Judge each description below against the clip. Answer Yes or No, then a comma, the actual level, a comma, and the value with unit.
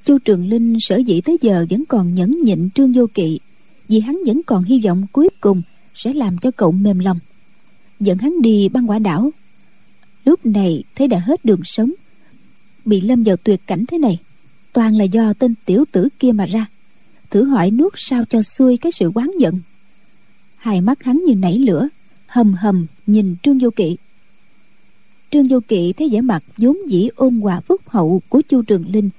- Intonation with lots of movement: No, average, 4.8 semitones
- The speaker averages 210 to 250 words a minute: No, average, 195 wpm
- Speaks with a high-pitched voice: Yes, high, 220 Hz